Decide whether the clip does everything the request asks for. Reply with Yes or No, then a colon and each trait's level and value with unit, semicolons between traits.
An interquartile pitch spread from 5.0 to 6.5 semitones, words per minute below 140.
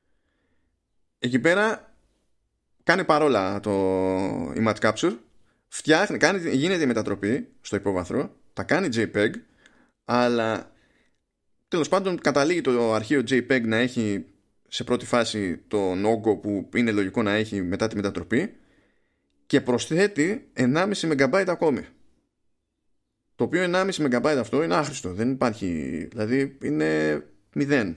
Yes: wide, 5.6 semitones; average, 120 wpm